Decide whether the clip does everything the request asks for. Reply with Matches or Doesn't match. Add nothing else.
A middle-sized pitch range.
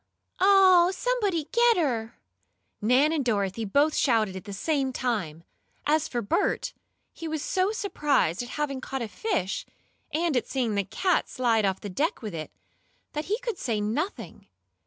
Doesn't match